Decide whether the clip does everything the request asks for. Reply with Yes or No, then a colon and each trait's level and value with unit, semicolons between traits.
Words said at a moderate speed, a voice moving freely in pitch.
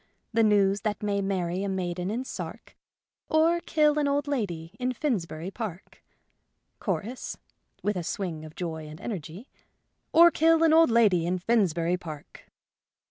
Yes: average, 155 wpm; wide, 6.5 semitones